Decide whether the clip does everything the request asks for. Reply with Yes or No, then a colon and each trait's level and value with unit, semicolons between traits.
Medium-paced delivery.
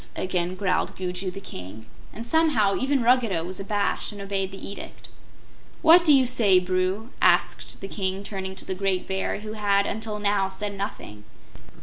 Yes: average, 170 wpm